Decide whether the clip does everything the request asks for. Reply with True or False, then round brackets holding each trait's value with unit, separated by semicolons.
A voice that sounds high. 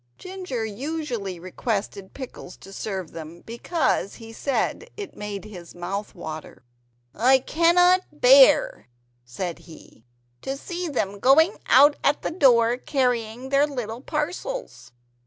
True (250 Hz)